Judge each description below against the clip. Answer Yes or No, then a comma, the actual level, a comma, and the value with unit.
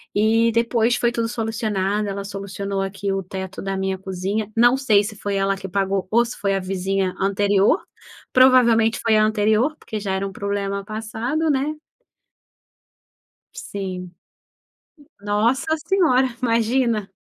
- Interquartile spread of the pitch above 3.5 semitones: No, average, 3.0 semitones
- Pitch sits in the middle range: No, high, 210 Hz